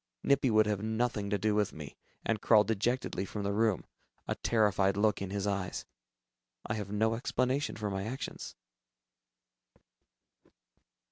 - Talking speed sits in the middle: Yes, average, 145 wpm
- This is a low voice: Yes, low, 105 Hz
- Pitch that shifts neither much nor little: No, narrow, 2.0 semitones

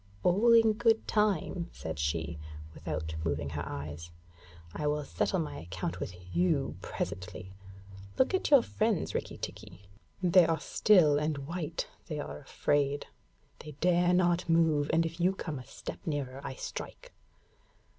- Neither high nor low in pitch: Yes, medium, 155 Hz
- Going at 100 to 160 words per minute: Yes, average, 150 wpm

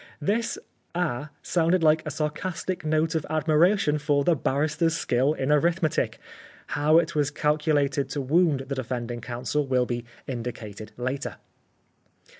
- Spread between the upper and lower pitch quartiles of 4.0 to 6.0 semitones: No, average, 3.4 semitones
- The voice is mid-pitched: Yes, medium, 150 Hz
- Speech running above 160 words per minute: No, average, 150 wpm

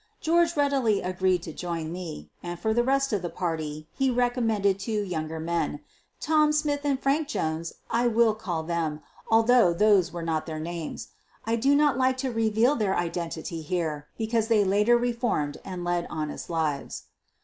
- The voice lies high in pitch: Yes, high, 195 Hz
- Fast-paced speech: No, average, 180 wpm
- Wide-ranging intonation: Yes, wide, 6.6 semitones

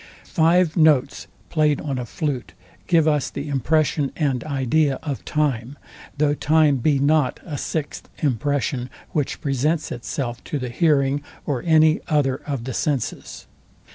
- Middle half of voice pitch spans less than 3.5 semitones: Yes, average, 2.7 semitones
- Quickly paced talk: No, average, 140 wpm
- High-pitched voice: No, medium, 145 Hz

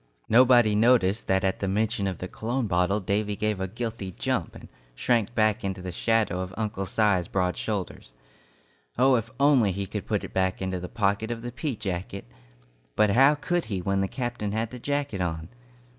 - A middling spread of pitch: Yes, average, 3.7 semitones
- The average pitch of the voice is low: Yes, low, 105 Hz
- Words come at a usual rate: Yes, average, 195 wpm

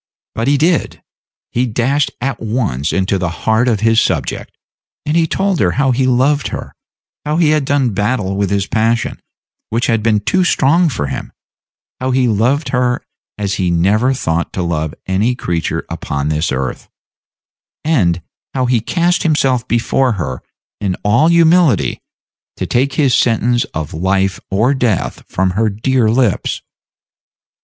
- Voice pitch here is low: Yes, low, 115 Hz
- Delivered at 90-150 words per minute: No, average, 160 wpm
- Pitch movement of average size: No, wide, 5.7 semitones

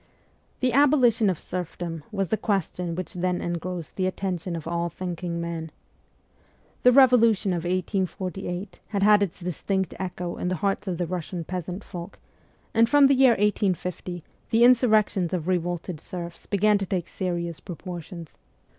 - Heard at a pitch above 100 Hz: Yes, medium, 185 Hz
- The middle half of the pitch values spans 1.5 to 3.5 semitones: Yes, average, 3.0 semitones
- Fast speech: No, average, 155 wpm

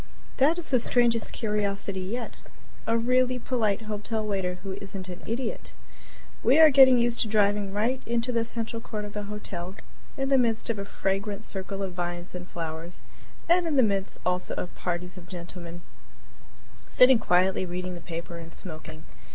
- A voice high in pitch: Yes, high, 205 Hz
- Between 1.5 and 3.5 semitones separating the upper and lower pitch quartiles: No, average, 4.5 semitones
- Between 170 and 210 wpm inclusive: Yes, average, 175 wpm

